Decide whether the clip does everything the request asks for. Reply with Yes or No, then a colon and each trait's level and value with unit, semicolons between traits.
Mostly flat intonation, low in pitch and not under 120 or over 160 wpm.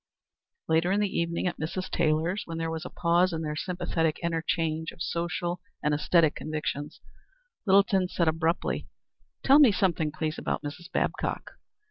No: narrow, 2.2 semitones; medium, 165 Hz; average, 155 wpm